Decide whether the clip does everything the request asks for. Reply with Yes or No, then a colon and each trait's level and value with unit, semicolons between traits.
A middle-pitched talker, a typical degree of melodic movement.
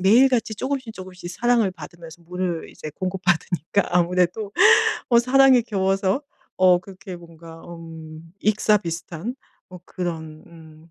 Yes: medium, 180 Hz; average, 4.1 semitones